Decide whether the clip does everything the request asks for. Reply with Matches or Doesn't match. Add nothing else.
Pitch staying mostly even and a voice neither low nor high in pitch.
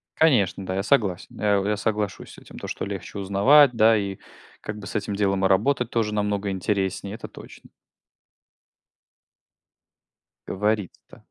Doesn't match